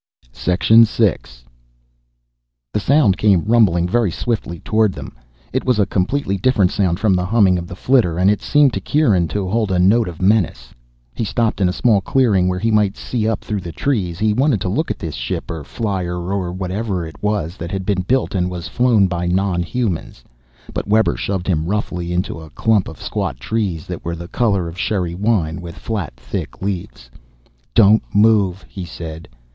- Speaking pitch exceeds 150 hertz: No, very low, 95 Hz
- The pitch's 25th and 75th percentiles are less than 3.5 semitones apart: No, average, 3.8 semitones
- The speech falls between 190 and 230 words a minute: Yes, average, 195 wpm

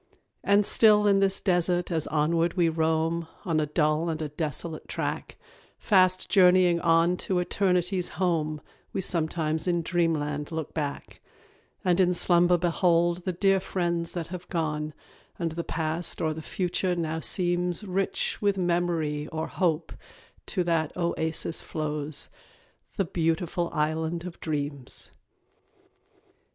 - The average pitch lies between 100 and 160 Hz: No, medium, 170 Hz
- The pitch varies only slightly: Yes, narrow, 2.2 semitones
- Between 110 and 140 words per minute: Yes, slow, 135 wpm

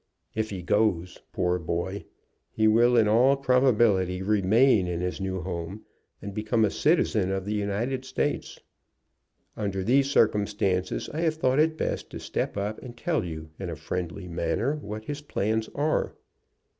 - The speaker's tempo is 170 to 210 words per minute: No, average, 160 wpm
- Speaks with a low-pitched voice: Yes, low, 105 Hz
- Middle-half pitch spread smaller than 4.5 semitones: No, average, 4.9 semitones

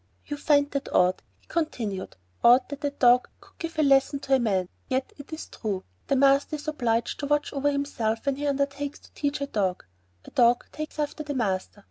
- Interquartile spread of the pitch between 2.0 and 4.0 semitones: Yes, average, 3.4 semitones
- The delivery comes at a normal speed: No, fast, 210 wpm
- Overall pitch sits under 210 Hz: No, very high, 275 Hz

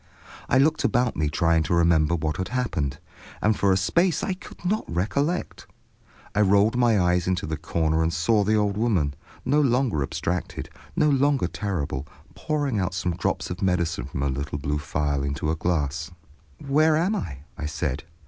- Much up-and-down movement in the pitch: Yes, wide, 7.7 semitones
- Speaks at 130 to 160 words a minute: No, average, 180 wpm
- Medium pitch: No, very low, 90 Hz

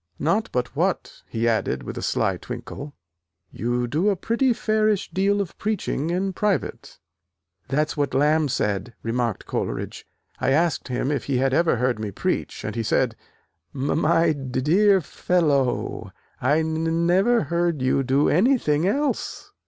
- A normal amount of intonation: No, wide, 6.4 semitones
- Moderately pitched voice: Yes, medium, 155 Hz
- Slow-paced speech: No, average, 160 wpm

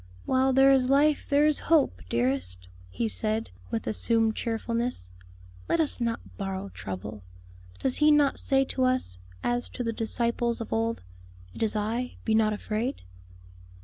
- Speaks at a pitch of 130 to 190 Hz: No, high, 230 Hz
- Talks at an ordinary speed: Yes, average, 155 wpm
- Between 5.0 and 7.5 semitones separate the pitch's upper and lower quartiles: Yes, wide, 5.6 semitones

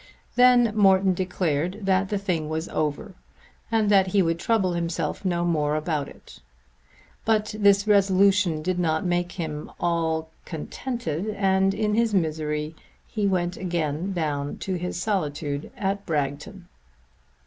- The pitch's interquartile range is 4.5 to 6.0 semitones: No, average, 3.9 semitones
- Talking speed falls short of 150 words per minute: Yes, average, 140 wpm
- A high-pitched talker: No, medium, 180 Hz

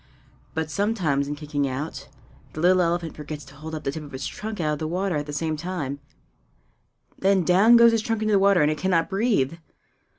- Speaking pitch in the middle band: Yes, medium, 160 Hz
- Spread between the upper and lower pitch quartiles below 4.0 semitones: No, average, 4.7 semitones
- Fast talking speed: Yes, fast, 220 wpm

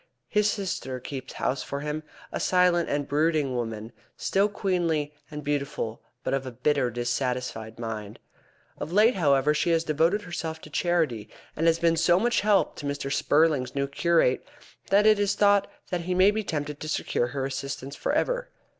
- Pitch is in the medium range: Yes, medium, 150 Hz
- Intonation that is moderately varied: Yes, average, 4.9 semitones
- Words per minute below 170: No, average, 180 wpm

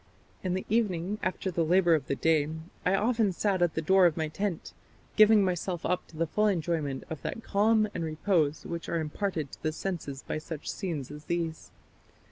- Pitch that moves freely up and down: No, average, 3.6 semitones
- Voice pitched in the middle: Yes, medium, 170 Hz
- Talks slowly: No, average, 200 wpm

